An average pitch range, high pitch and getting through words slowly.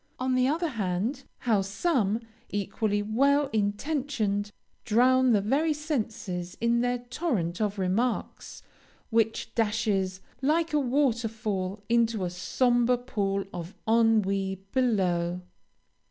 Yes: average, 4.3 semitones; high, 225 Hz; slow, 115 wpm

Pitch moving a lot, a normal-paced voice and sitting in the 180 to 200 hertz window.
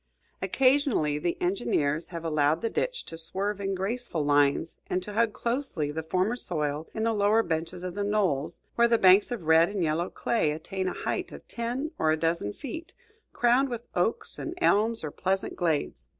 Yes: wide, 6.2 semitones; average, 190 wpm; medium, 185 Hz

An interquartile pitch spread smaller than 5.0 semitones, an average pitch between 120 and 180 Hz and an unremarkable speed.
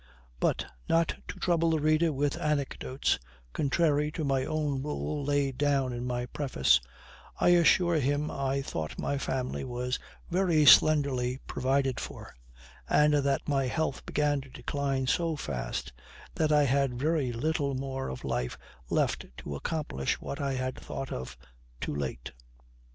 Yes: average, 2.7 semitones; medium, 140 Hz; average, 150 wpm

